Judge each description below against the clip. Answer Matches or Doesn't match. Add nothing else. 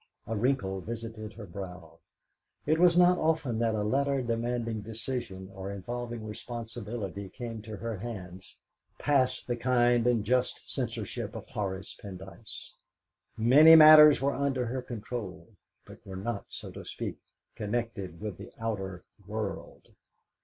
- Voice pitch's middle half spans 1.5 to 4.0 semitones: Matches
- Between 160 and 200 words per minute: Doesn't match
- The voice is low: Matches